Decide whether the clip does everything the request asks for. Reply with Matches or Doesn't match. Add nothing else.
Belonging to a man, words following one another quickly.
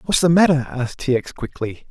Matches